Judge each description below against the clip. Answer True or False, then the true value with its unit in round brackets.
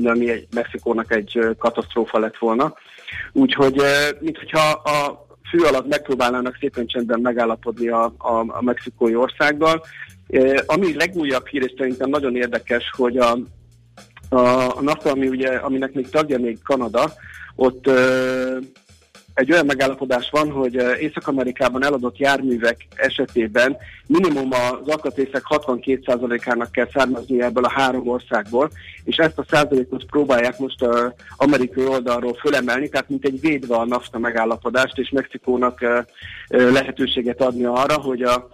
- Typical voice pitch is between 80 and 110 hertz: False (125 Hz)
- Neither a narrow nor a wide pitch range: False (2.2 semitones)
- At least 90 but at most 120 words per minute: False (130 wpm)